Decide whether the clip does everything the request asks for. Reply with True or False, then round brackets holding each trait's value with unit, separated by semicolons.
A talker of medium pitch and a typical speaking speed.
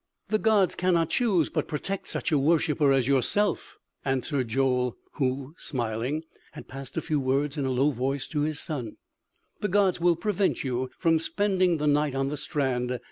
True (145 Hz; 180 wpm)